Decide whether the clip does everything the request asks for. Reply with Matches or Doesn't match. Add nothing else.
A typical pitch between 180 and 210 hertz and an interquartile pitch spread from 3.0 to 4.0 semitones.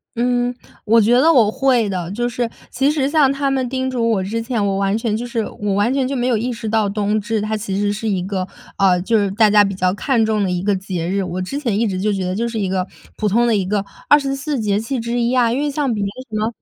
Doesn't match